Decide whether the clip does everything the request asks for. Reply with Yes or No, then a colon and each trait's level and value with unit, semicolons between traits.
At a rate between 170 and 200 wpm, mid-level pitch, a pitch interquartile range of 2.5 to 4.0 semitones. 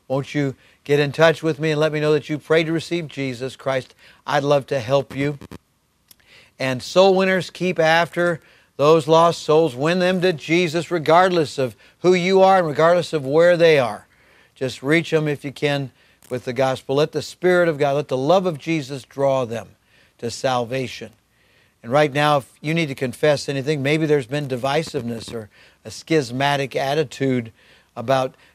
Yes: average, 185 wpm; medium, 145 Hz; average, 3.6 semitones